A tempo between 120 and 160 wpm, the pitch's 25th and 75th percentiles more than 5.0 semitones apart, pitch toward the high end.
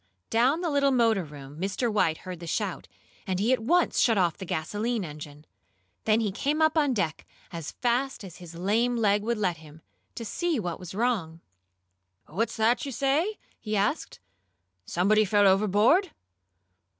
No: average, 175 wpm; wide, 5.6 semitones; high, 210 Hz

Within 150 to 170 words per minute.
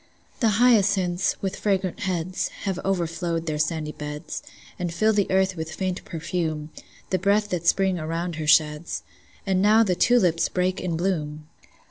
Yes: average, 155 wpm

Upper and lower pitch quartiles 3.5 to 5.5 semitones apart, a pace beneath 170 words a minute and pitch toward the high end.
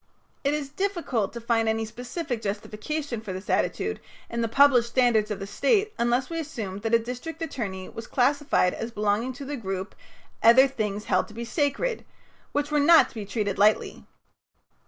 No: average, 5.0 semitones; average, 180 wpm; high, 235 Hz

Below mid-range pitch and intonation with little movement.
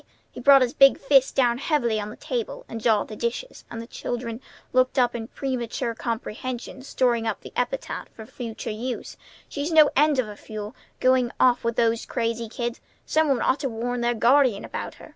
No: high, 240 Hz; narrow, 2.3 semitones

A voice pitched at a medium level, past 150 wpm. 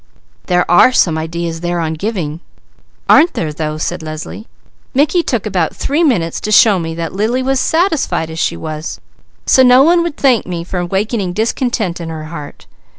Yes: medium, 180 Hz; average, 180 wpm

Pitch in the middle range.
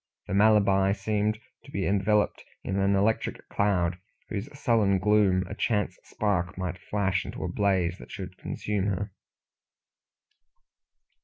No: low, 100 Hz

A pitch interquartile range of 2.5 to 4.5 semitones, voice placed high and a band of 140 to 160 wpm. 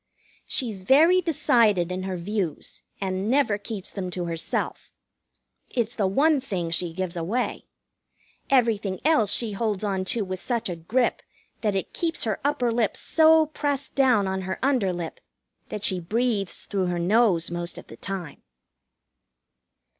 No: average, 4.9 semitones; high, 205 Hz; average, 155 wpm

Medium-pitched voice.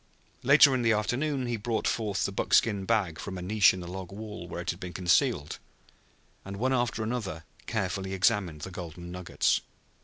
No: low, 100 Hz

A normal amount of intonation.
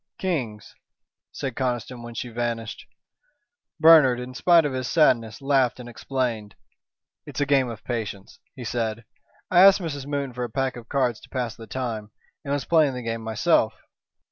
Yes: average, 3.3 semitones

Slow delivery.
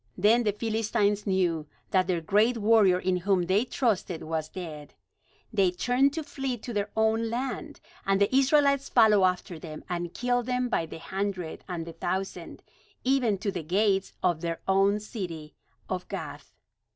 No: average, 165 wpm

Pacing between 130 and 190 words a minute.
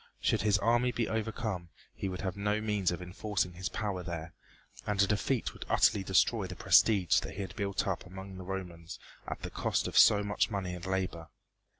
No: fast, 205 wpm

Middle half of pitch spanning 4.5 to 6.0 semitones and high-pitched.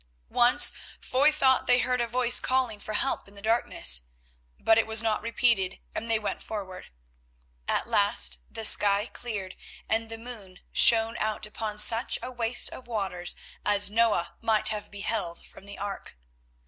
No: narrow, 2.6 semitones; high, 220 Hz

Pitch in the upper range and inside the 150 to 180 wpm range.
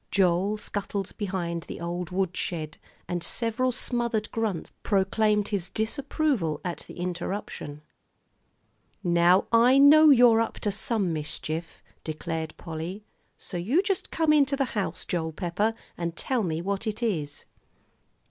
No: high, 195 Hz; slow, 135 wpm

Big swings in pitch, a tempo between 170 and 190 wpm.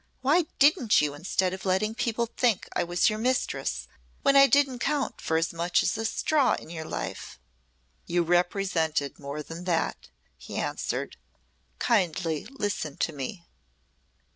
No: wide, 6.6 semitones; average, 150 wpm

